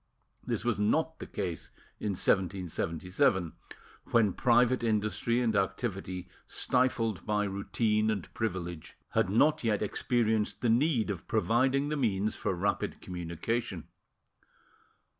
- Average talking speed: No, slow, 120 wpm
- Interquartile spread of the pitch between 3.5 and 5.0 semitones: Yes, average, 3.8 semitones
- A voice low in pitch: Yes, low, 105 Hz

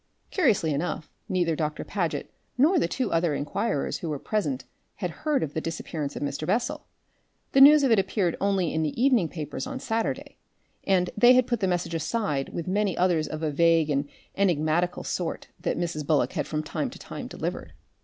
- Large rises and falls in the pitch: Yes, wide, 5.7 semitones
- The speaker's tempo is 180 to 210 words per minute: Yes, average, 195 wpm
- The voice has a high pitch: No, medium, 175 Hz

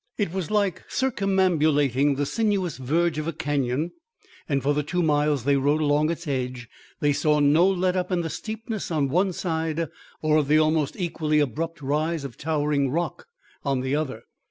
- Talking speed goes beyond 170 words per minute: Yes, average, 180 wpm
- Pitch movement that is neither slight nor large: Yes, average, 3.3 semitones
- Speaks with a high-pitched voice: No, medium, 155 Hz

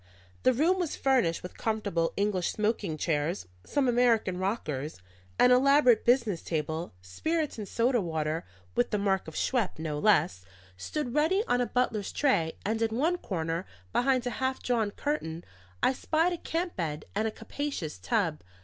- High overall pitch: Yes, high, 220 Hz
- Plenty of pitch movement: Yes, wide, 7.8 semitones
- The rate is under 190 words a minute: Yes, average, 170 wpm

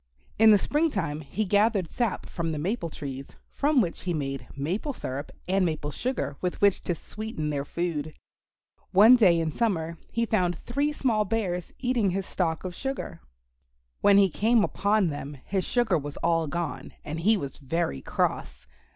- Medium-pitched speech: Yes, medium, 180 Hz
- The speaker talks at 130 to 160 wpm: No, average, 175 wpm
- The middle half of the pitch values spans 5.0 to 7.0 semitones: Yes, wide, 5.6 semitones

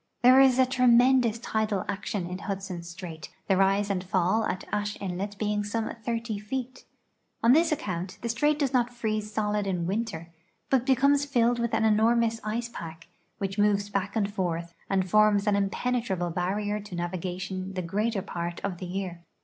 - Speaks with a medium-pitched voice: No, high, 205 Hz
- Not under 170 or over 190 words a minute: Yes, average, 180 wpm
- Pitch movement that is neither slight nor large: Yes, average, 3.8 semitones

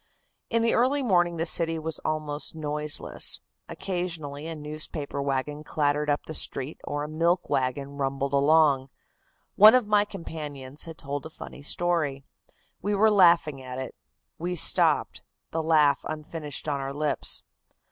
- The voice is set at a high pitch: No, medium, 155 Hz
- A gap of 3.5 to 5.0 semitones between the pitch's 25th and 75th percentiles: No, average, 3.1 semitones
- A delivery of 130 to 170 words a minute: Yes, average, 150 wpm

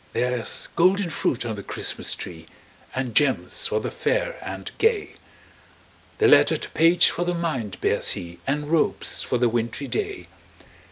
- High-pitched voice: No, medium, 145 Hz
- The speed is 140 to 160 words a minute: Yes, average, 155 wpm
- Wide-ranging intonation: Yes, wide, 7.0 semitones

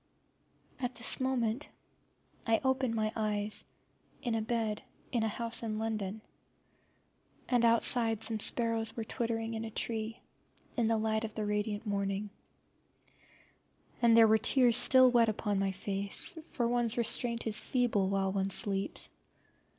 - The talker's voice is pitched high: Yes, high, 225 Hz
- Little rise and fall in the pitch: Yes, narrow, 1.9 semitones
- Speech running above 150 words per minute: No, average, 145 wpm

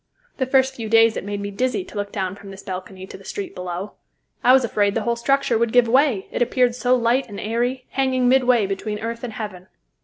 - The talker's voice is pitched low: No, high, 230 Hz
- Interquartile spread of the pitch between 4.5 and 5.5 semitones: No, average, 3.9 semitones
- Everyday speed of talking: No, fast, 235 wpm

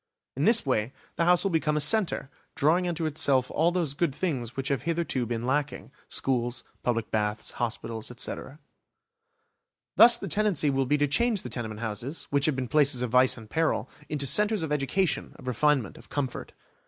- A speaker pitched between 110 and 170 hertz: Yes, medium, 140 Hz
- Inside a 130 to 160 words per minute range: No, average, 185 wpm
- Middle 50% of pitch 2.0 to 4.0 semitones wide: No, average, 4.8 semitones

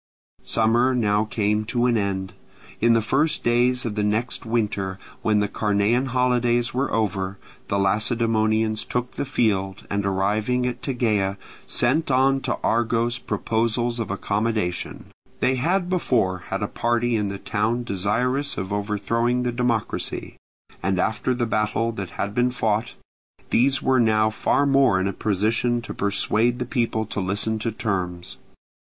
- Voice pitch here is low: Yes, low, 110 Hz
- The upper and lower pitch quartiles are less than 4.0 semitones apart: Yes, average, 3.1 semitones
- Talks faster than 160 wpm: No, average, 155 wpm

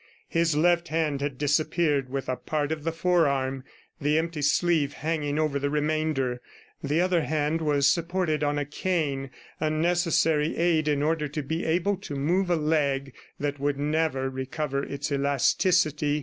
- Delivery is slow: No, average, 165 wpm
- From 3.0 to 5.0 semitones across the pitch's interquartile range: No, narrow, 2.5 semitones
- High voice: No, medium, 150 Hz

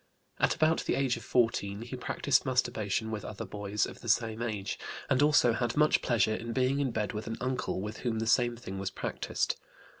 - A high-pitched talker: No, low, 115 Hz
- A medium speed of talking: No, fast, 210 wpm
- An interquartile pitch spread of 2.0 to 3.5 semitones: Yes, average, 3.1 semitones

